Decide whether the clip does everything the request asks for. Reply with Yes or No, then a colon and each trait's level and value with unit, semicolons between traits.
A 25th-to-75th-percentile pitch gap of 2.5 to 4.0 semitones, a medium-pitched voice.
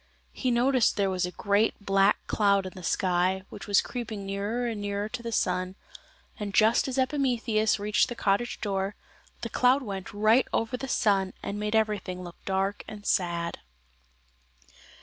No: average, 3.0 semitones; high, 205 Hz